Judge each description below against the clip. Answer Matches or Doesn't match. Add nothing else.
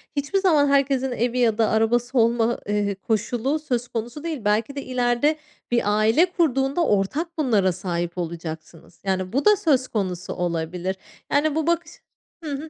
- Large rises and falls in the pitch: Matches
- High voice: Matches